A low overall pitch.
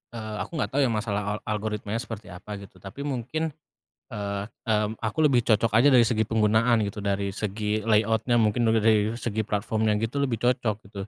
Yes: low, 110 Hz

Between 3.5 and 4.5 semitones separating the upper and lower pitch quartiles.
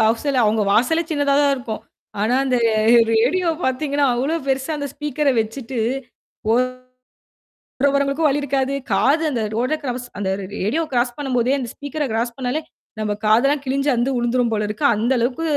No: average, 3.1 semitones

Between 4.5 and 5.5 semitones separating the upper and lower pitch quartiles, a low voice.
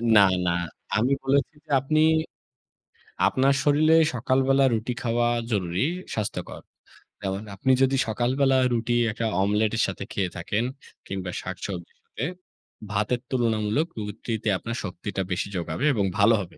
Yes: average, 4.8 semitones; low, 115 Hz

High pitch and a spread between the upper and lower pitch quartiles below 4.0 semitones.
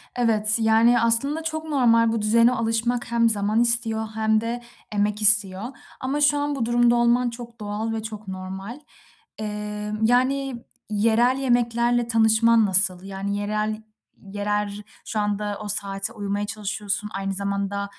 Yes: high, 220 Hz; narrow, 2.4 semitones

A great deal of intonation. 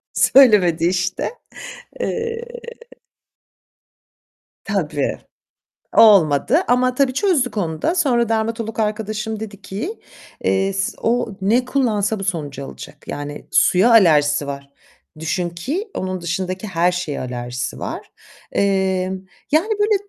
Yes: wide, 6.0 semitones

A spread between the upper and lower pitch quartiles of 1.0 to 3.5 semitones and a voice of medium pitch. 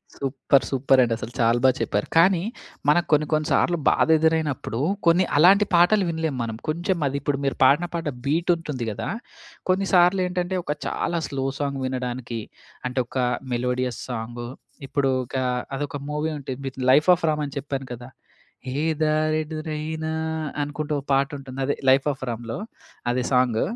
No: average, 3.9 semitones; medium, 145 Hz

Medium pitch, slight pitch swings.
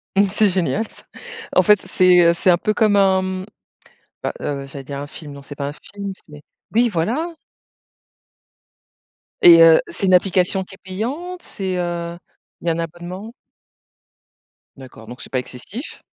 No: medium, 180 Hz; average, 4.0 semitones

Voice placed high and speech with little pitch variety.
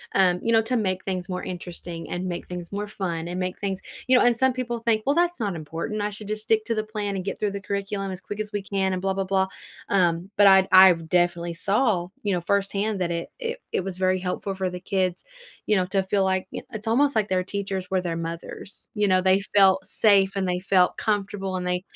Yes: high, 195 Hz; narrow, 2.3 semitones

